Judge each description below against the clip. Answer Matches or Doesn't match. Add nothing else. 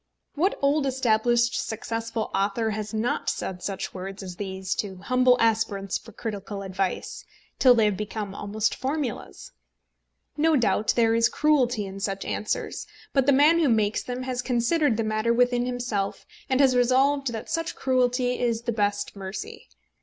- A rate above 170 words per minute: Doesn't match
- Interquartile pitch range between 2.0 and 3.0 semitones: Doesn't match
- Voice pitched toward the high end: Matches